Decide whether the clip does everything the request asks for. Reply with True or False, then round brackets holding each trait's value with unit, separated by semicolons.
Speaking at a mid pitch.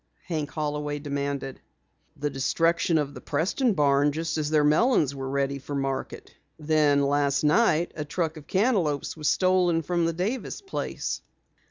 True (150 Hz)